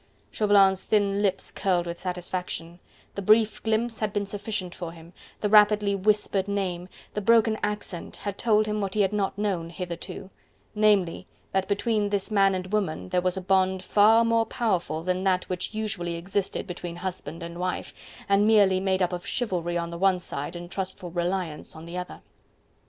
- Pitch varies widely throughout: No, average, 2.8 semitones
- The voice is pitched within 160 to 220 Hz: Yes, high, 190 Hz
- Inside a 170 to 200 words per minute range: Yes, average, 180 wpm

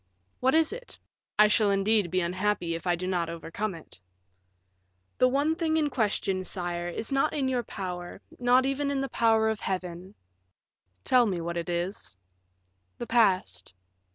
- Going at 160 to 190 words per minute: Yes, average, 165 wpm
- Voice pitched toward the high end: Yes, high, 205 Hz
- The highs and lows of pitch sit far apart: Yes, wide, 6.3 semitones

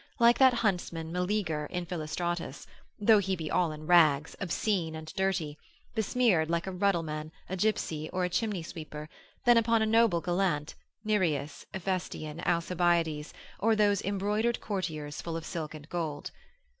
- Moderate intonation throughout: Yes, average, 4.2 semitones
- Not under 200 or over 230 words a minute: No, average, 150 wpm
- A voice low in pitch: No, medium, 175 Hz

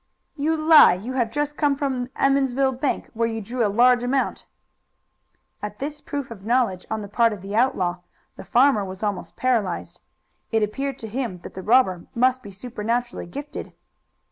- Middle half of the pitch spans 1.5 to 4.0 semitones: No, average, 4.4 semitones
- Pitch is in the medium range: No, high, 240 Hz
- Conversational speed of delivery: Yes, average, 180 wpm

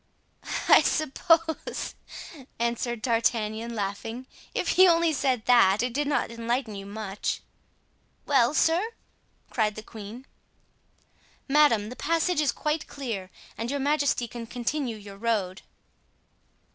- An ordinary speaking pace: No, slow, 125 wpm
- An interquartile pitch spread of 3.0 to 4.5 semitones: No, average, 5.0 semitones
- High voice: Yes, high, 240 Hz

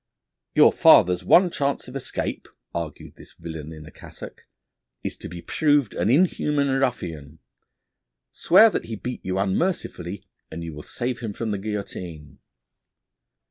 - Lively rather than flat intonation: Yes, wide, 8.3 semitones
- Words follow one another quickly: No, average, 145 wpm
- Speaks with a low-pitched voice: Yes, low, 100 Hz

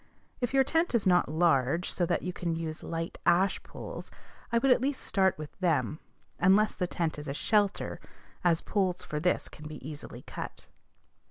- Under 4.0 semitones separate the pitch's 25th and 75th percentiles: No, average, 4.3 semitones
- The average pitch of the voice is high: No, medium, 175 Hz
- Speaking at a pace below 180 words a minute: No, average, 185 wpm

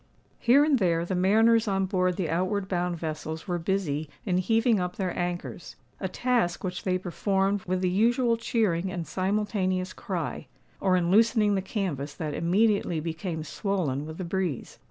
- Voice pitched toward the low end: No, medium, 185 Hz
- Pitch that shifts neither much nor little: Yes, average, 3.0 semitones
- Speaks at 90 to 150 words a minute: No, average, 160 wpm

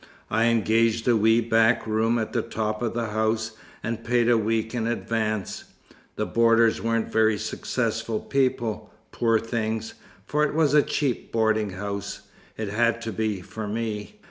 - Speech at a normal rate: Yes, average, 165 wpm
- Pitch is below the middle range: Yes, low, 115 Hz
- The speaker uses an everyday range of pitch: No, narrow, 1.2 semitones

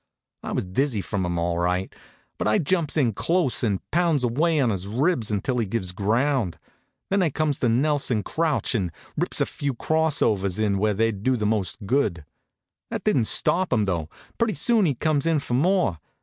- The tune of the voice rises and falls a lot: Yes, wide, 7.3 semitones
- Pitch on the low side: Yes, low, 120 Hz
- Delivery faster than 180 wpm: Yes, average, 195 wpm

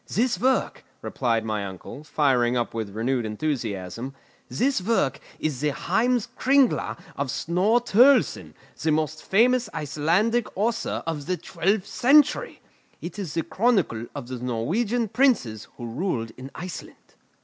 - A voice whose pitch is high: No, medium, 160 Hz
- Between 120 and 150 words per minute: Yes, average, 140 wpm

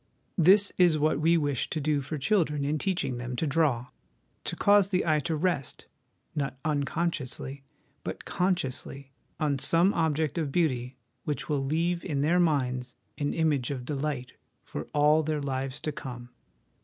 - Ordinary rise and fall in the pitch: Yes, average, 3.4 semitones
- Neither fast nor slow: Yes, average, 165 wpm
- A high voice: No, medium, 150 Hz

